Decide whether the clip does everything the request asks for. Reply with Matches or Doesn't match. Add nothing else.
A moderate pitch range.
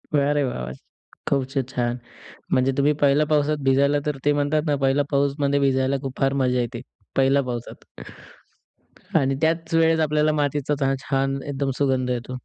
Doesn't match